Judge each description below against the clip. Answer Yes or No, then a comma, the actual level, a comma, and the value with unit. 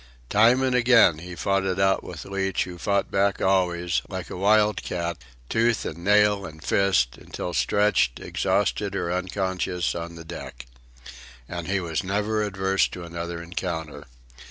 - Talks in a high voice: No, very low, 95 Hz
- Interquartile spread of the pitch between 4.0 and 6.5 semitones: No, average, 2.8 semitones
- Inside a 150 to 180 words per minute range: Yes, average, 155 wpm